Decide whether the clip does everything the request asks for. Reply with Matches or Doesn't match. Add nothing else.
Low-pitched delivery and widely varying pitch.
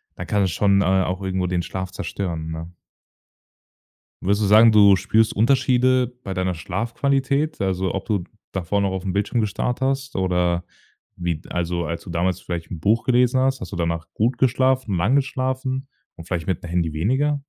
Matches